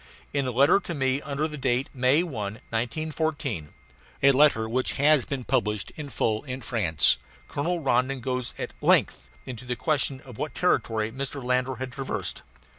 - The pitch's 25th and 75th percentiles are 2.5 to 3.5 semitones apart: Yes, average, 3.0 semitones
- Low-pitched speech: Yes, low, 130 Hz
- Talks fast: No, average, 170 wpm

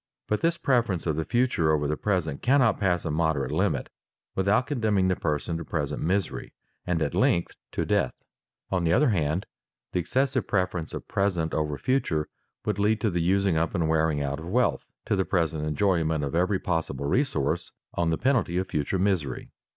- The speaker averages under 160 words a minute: No, average, 190 wpm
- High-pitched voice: No, very low, 85 Hz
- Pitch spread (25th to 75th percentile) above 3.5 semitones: Yes, average, 4.4 semitones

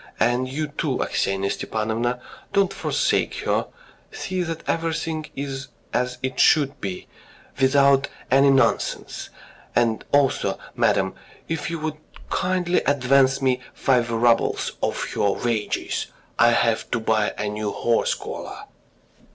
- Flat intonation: No, average, 4.1 semitones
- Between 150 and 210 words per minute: No, slow, 135 wpm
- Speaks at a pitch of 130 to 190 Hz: Yes, low, 135 Hz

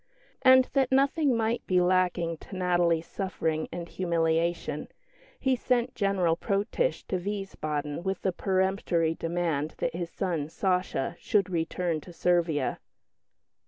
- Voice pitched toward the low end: No, medium, 180 Hz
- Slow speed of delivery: Yes, slow, 125 wpm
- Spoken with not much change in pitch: No, average, 3.1 semitones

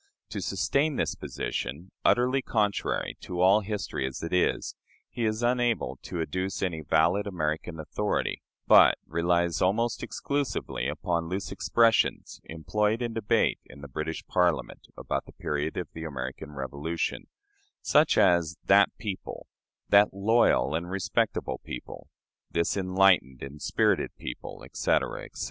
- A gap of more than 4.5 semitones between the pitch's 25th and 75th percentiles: Yes, average, 5.0 semitones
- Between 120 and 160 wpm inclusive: Yes, slow, 135 wpm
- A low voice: Yes, very low, 90 Hz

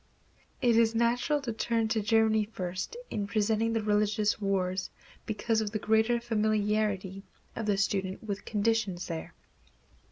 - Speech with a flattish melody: Yes, narrow, 1.9 semitones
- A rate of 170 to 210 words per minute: No, average, 140 wpm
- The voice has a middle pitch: No, high, 215 Hz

